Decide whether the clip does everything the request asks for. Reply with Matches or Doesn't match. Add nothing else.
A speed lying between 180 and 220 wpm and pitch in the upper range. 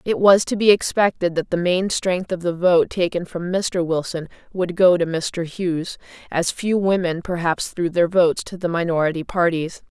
Doesn't match